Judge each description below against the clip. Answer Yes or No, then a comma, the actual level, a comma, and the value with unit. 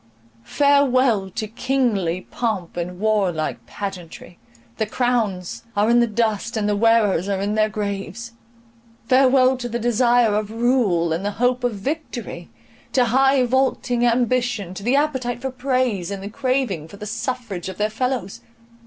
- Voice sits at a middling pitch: No, high, 230 Hz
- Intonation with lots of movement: No, average, 3.8 semitones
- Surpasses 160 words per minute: No, average, 155 wpm